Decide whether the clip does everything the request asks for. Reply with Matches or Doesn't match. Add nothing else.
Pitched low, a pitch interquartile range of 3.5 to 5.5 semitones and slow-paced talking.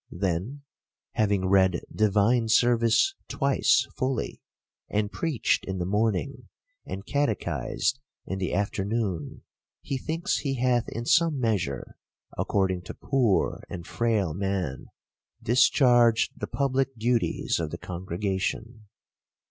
Matches